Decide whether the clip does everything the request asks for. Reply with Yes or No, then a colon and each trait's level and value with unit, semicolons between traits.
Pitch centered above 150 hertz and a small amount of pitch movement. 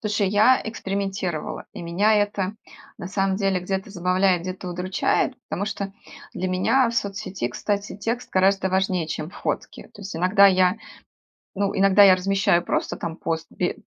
Yes: high, 190 Hz; narrow, 1.8 semitones